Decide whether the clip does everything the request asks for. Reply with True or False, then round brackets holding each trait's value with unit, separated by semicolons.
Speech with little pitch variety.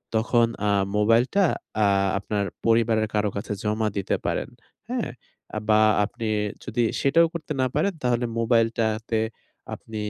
True (2.1 semitones)